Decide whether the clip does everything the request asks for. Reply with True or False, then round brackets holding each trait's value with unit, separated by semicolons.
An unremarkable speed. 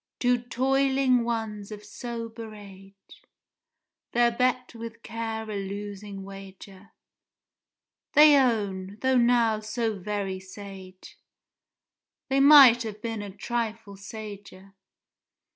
False (105 wpm)